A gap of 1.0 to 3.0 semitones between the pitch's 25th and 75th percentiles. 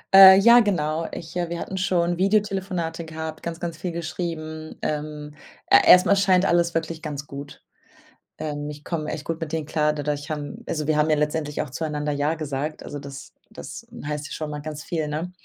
Yes: narrow, 2.4 semitones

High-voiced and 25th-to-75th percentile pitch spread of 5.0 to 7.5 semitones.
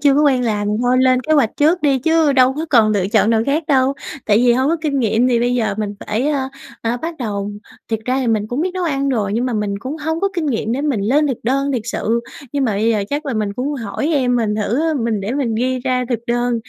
No: very high, 250 Hz; average, 4.1 semitones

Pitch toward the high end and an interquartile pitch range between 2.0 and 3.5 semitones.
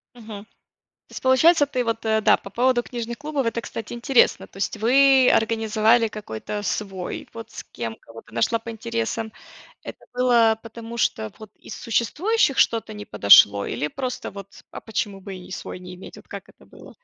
Yes: high, 225 Hz; average, 3.0 semitones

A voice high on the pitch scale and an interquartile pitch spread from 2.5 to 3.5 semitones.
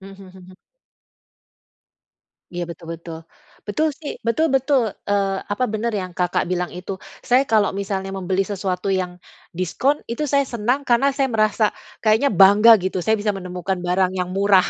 No: high, 195 Hz; average, 4.1 semitones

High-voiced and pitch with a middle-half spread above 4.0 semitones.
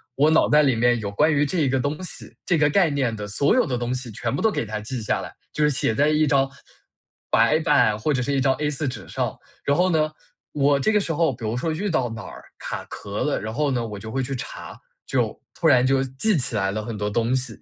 No: low, 135 Hz; average, 4.4 semitones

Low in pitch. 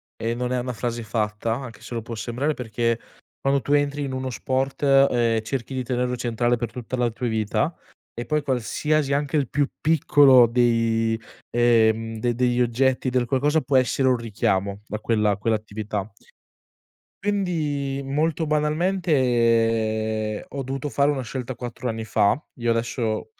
Yes: low, 125 Hz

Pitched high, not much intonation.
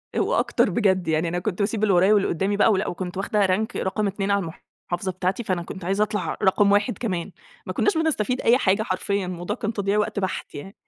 Yes: high, 195 Hz; narrow, 2.3 semitones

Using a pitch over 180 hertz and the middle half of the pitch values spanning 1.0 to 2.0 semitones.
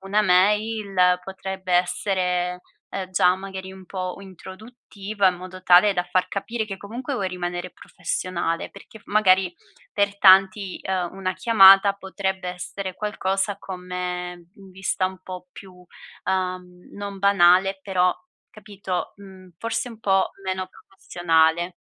Yes: high, 190 Hz; narrow, 1.6 semitones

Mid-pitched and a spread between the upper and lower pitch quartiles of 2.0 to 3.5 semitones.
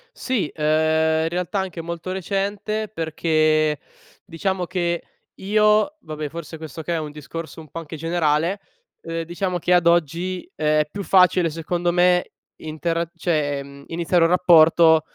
Yes: medium, 165 Hz; narrow, 2.5 semitones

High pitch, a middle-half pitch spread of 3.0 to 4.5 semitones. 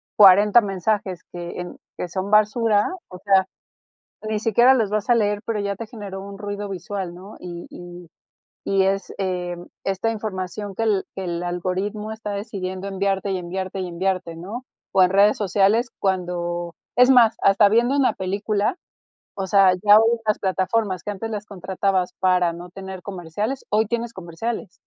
No: high, 195 Hz; narrow, 2.6 semitones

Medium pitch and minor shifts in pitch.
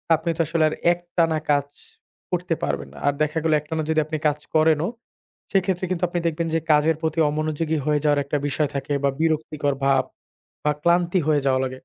Yes: medium, 155 Hz; narrow, 2.1 semitones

